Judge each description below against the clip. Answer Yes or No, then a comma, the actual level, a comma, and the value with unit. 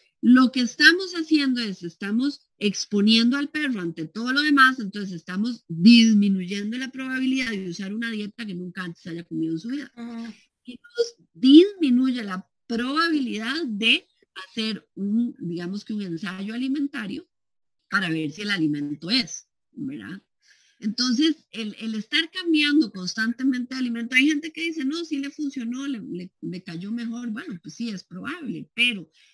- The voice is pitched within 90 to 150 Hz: No, high, 235 Hz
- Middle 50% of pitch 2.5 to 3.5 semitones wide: No, wide, 5.4 semitones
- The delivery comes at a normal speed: Yes, average, 155 wpm